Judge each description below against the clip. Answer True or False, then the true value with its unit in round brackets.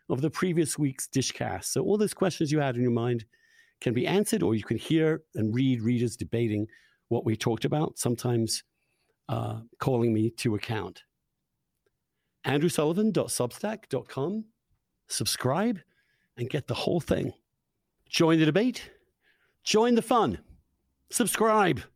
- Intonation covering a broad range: True (7.8 semitones)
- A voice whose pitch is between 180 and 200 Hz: False (140 Hz)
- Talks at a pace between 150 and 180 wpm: False (135 wpm)